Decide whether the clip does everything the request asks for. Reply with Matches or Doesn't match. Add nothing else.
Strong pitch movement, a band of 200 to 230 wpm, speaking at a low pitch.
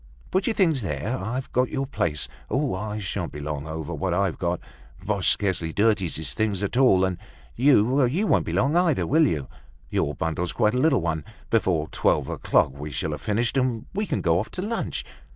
Matches